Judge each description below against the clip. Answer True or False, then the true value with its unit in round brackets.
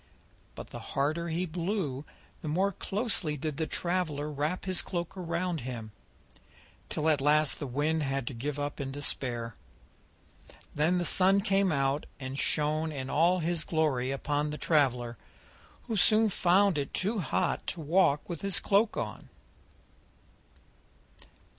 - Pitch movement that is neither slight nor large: True (4.3 semitones)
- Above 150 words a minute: False (145 wpm)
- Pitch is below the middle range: False (155 Hz)